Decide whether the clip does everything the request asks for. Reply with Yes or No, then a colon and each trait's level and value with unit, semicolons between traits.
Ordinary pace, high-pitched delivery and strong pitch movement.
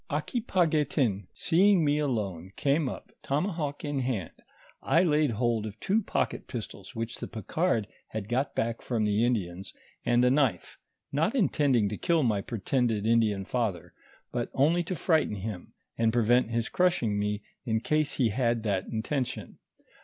No: average, 155 wpm; low, 120 Hz; wide, 5.7 semitones